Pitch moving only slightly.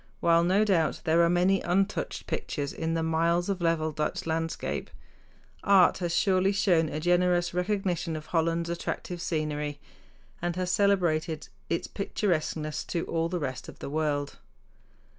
Yes: narrow, 2.2 semitones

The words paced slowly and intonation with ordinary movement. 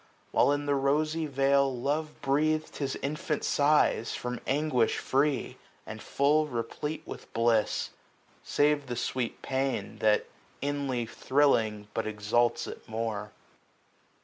Yes: slow, 125 wpm; average, 3.9 semitones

